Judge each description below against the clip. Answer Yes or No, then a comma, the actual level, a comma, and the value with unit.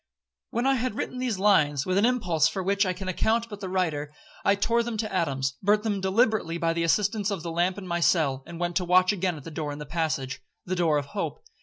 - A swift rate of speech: Yes, fast, 250 wpm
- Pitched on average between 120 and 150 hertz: No, medium, 185 Hz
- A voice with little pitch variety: No, average, 4.1 semitones